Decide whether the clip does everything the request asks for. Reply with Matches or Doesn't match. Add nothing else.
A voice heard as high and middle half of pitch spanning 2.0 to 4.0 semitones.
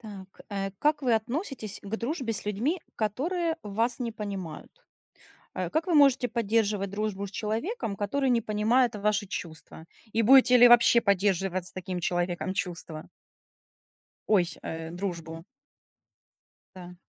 Doesn't match